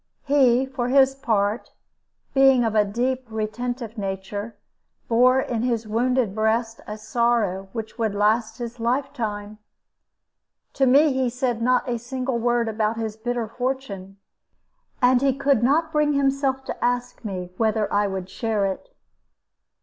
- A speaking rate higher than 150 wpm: No, average, 145 wpm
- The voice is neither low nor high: No, high, 235 Hz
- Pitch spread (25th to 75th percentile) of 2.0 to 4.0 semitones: Yes, average, 3.2 semitones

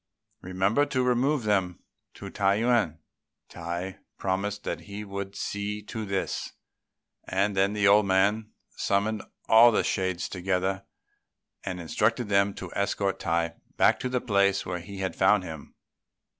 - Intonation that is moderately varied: No, narrow, 2.0 semitones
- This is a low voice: Yes, low, 100 Hz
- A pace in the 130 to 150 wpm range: Yes, average, 145 wpm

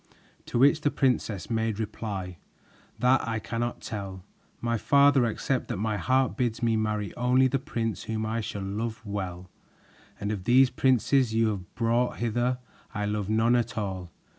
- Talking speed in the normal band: Yes, average, 165 wpm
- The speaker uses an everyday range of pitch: Yes, average, 3.0 semitones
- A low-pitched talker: Yes, low, 115 Hz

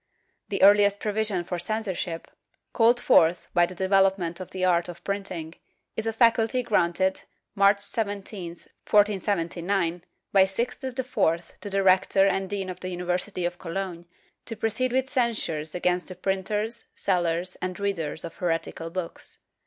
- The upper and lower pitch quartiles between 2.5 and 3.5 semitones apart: Yes, average, 2.9 semitones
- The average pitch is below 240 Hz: Yes, high, 190 Hz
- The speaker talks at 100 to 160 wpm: Yes, average, 150 wpm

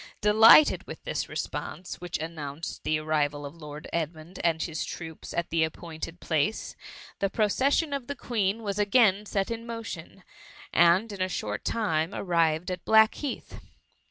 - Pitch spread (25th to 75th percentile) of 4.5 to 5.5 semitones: Yes, average, 5.2 semitones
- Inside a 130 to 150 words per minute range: No, average, 160 wpm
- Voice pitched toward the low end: No, medium, 180 Hz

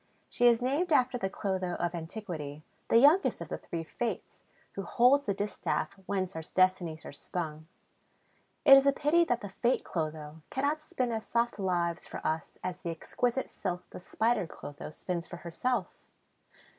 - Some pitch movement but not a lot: No, wide, 6.4 semitones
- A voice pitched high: Yes, high, 195 Hz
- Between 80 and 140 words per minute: No, average, 170 wpm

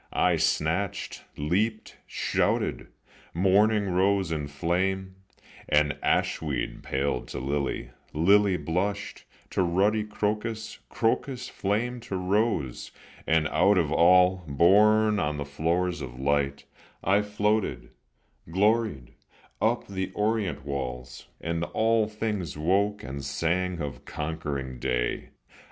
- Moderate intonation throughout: No, wide, 5.8 semitones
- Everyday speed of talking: No, slow, 110 wpm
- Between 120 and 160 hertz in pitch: No, very low, 90 Hz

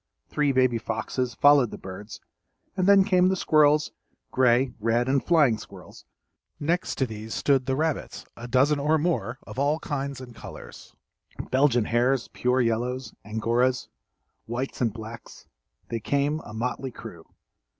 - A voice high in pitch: No, low, 130 Hz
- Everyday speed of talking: Yes, average, 150 wpm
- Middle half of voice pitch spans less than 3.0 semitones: No, average, 3.8 semitones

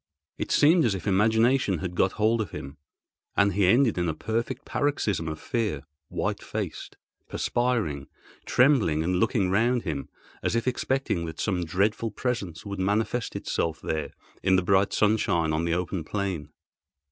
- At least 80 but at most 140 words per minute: No, average, 160 wpm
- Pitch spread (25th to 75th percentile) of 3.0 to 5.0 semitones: No, wide, 5.5 semitones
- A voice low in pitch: Yes, low, 100 Hz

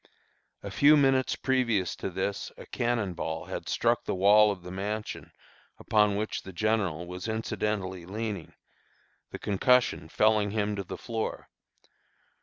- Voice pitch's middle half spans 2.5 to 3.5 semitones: Yes, average, 2.9 semitones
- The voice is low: Yes, low, 105 Hz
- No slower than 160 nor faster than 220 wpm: No, average, 145 wpm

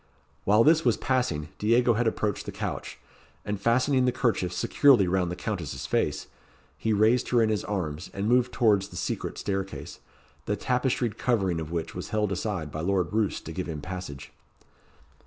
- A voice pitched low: Yes, low, 105 Hz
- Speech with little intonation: No, average, 4.8 semitones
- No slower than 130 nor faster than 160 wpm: No, average, 175 wpm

